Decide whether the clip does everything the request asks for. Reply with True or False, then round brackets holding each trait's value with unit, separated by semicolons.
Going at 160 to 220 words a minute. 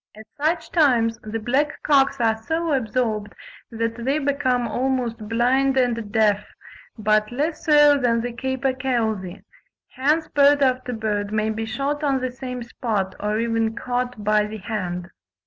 False (150 wpm)